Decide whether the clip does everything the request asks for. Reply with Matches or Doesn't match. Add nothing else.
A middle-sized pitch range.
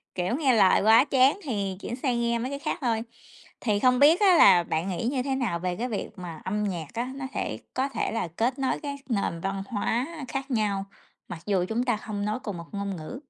Matches